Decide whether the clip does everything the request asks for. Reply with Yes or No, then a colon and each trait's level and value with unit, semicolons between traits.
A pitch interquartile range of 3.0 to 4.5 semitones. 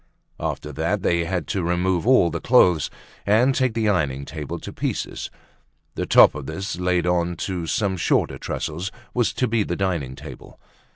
Yes: average, 3.6 semitones